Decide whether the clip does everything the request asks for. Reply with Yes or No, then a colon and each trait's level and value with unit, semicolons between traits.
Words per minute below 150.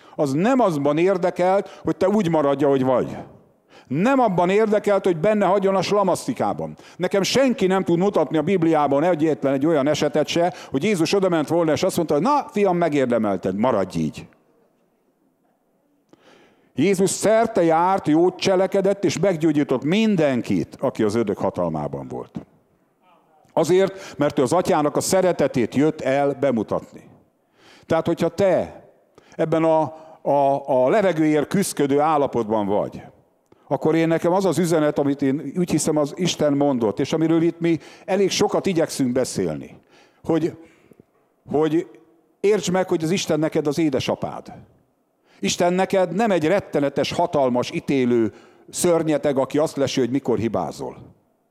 Yes: average, 140 wpm